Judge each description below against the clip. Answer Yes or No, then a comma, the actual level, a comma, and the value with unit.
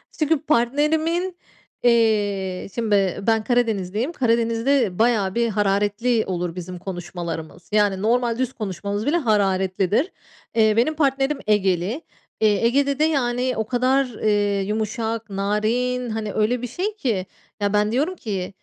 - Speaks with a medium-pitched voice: No, high, 220 Hz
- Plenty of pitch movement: No, average, 3.8 semitones